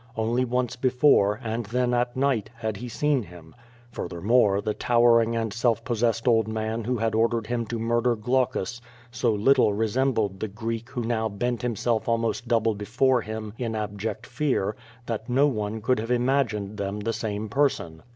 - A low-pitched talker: Yes, low, 115 Hz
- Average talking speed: Yes, average, 175 wpm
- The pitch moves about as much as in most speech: No, narrow, 2.2 semitones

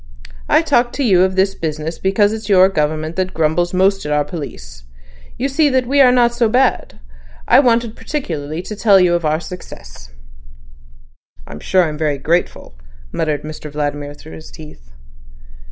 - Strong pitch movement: Yes, wide, 6.1 semitones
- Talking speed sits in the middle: Yes, average, 170 wpm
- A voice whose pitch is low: No, medium, 175 Hz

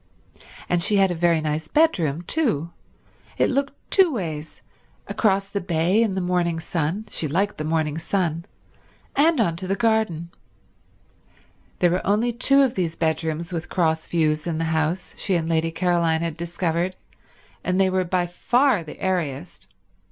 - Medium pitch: Yes, medium, 175 Hz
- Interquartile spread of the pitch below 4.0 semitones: Yes, average, 3.4 semitones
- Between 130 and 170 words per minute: Yes, average, 155 wpm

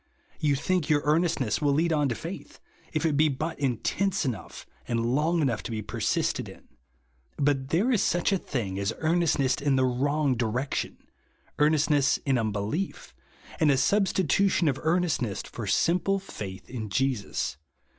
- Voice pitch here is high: No, medium, 145 Hz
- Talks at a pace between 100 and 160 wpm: Yes, average, 155 wpm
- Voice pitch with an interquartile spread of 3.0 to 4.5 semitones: No, average, 5.0 semitones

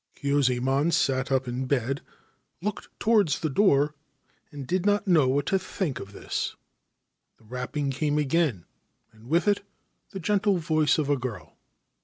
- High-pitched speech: No, medium, 145 Hz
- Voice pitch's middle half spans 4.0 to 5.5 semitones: Yes, average, 4.8 semitones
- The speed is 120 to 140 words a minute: No, average, 155 wpm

